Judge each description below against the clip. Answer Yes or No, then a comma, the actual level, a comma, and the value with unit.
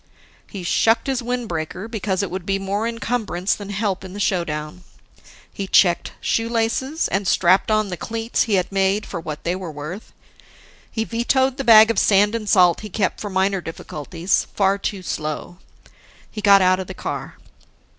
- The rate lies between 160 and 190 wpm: Yes, average, 175 wpm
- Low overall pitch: No, high, 195 Hz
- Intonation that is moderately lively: Yes, average, 3.5 semitones